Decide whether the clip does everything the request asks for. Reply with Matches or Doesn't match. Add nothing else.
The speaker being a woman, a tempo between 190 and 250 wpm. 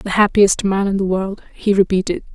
Matches